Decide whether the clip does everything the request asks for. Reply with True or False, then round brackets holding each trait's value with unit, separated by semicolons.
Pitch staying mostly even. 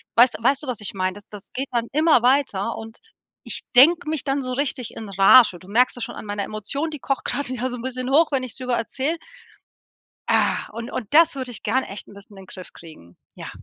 False (4.6 semitones)